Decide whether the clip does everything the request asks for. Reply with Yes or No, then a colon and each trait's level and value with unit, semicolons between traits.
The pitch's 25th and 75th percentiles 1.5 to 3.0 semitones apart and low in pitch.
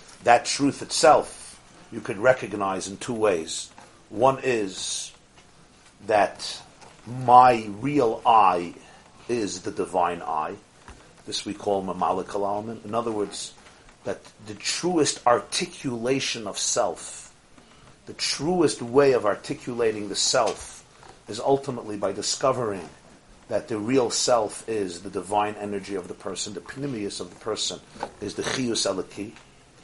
No: average, 4.7 semitones; low, 115 Hz